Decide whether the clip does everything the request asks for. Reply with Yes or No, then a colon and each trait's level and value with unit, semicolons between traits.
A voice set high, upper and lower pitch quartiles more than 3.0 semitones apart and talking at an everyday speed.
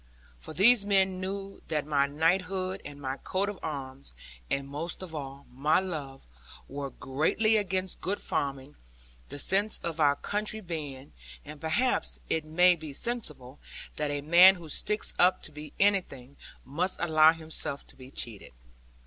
No: medium, 160 Hz; average, 5.0 semitones; average, 155 wpm